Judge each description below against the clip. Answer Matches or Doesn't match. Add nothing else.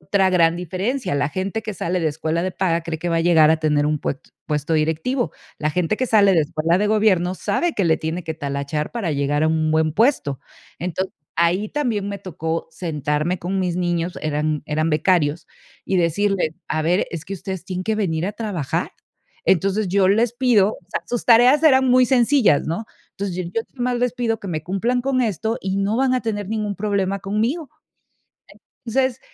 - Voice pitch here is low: Doesn't match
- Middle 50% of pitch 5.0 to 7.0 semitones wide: Matches